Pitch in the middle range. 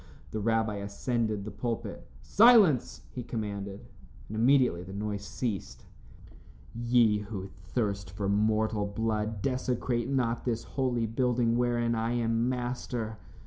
No: low, 115 Hz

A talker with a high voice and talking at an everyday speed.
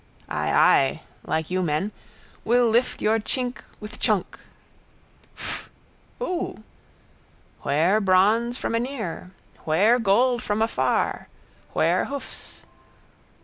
No: high, 215 Hz; slow, 105 wpm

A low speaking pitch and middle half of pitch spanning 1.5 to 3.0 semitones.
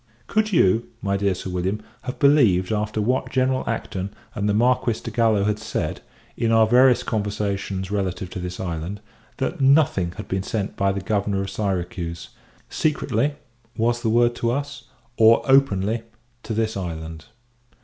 No: low, 105 Hz; average, 4.0 semitones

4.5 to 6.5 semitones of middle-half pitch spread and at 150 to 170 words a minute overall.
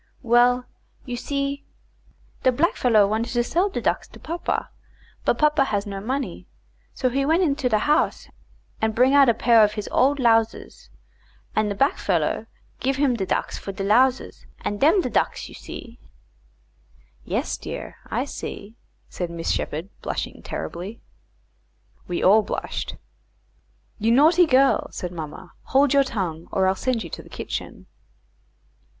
Yes: average, 5.2 semitones; average, 155 wpm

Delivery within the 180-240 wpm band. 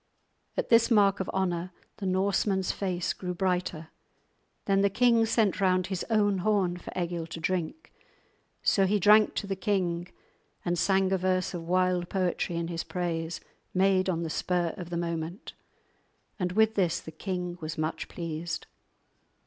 No: average, 165 wpm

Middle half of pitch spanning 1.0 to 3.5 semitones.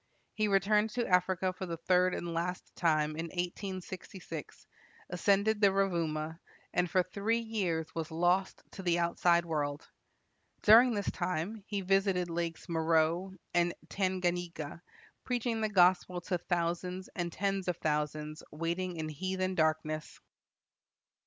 Yes: narrow, 2.6 semitones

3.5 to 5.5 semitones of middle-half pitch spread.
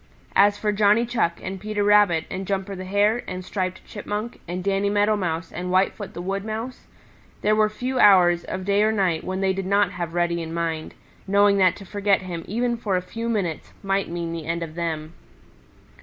No: average, 2.9 semitones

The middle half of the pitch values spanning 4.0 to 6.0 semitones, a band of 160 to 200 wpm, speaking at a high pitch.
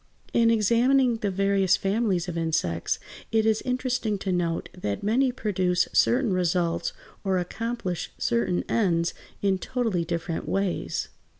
No: average, 4.5 semitones; slow, 135 wpm; high, 195 Hz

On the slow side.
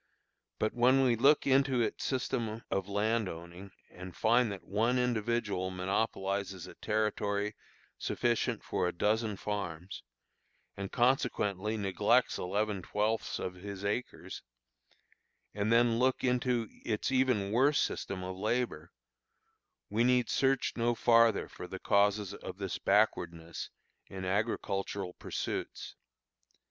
Yes: slow, 125 wpm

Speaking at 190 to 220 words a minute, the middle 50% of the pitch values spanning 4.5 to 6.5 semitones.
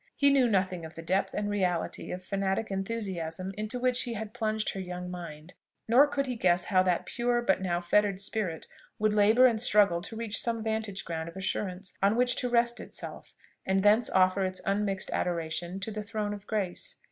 No: average, 200 wpm; average, 3.2 semitones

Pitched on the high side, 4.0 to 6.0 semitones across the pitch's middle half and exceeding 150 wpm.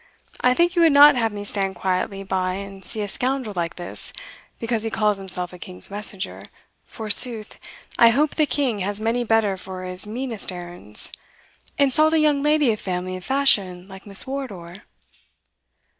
Yes: high, 210 Hz; wide, 5.5 semitones; average, 175 wpm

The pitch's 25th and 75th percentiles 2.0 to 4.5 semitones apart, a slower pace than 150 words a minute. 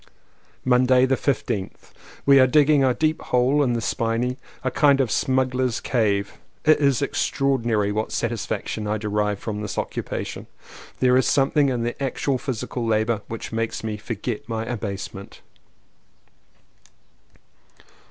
Yes: average, 3.4 semitones; average, 140 wpm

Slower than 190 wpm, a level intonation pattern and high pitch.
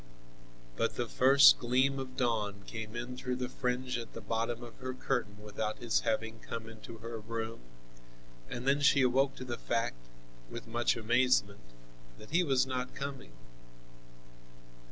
No: average, 155 wpm; narrow, 2.3 semitones; low, 120 Hz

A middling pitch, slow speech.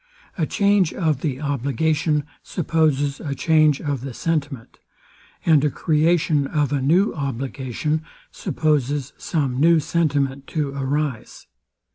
Yes: medium, 145 Hz; slow, 120 wpm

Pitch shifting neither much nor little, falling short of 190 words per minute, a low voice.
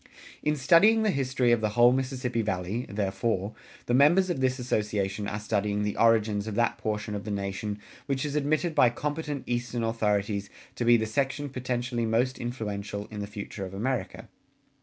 Yes: average, 4.0 semitones; average, 180 wpm; low, 115 Hz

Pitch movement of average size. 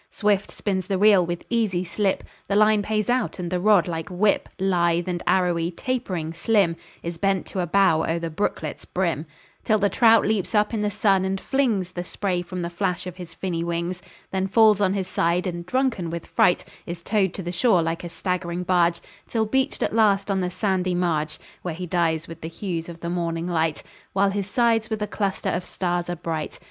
Yes: average, 3.0 semitones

